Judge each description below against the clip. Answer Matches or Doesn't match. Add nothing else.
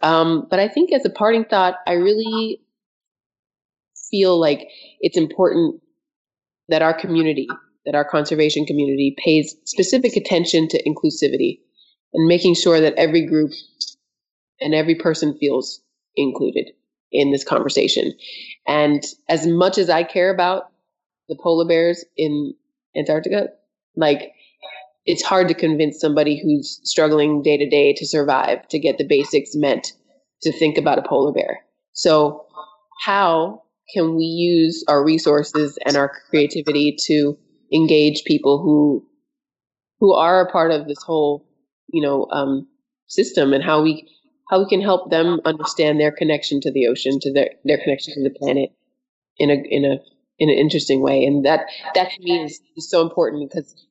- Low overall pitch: Doesn't match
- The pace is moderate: Matches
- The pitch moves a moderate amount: Matches